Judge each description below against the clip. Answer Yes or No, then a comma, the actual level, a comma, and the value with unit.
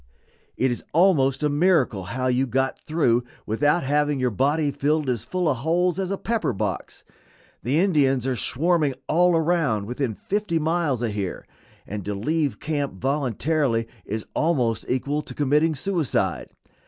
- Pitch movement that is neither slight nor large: Yes, average, 4.7 semitones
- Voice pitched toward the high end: No, medium, 145 Hz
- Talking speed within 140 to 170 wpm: Yes, average, 155 wpm